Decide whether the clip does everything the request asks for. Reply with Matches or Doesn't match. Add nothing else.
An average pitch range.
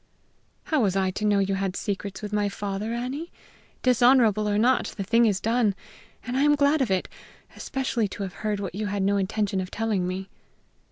Matches